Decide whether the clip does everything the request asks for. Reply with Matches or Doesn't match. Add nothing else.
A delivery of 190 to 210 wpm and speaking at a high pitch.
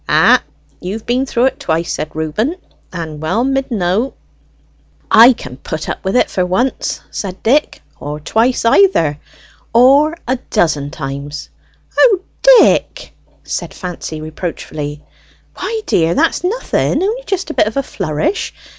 Doesn't match